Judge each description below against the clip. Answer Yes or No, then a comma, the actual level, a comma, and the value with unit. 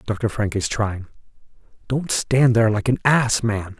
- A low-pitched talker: Yes, low, 115 Hz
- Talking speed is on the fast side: No, average, 175 wpm